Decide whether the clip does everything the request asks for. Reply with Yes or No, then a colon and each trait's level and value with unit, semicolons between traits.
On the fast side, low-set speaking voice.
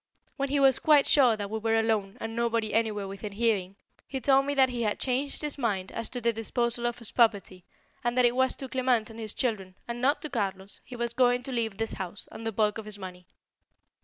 No: fast, 240 wpm; high, 230 Hz